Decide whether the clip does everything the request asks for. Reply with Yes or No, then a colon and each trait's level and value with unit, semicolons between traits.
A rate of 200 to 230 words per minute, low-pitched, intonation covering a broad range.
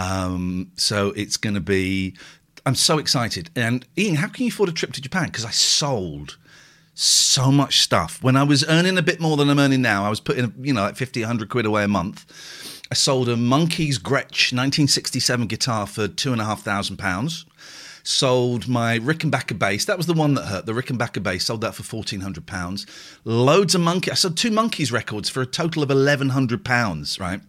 Yes: fast, 205 wpm; low, 125 Hz; wide, 5.8 semitones